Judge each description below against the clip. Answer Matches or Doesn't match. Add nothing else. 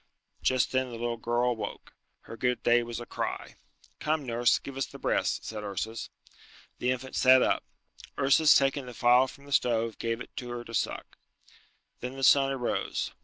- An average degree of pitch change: Doesn't match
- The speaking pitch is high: Doesn't match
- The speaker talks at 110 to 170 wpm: Doesn't match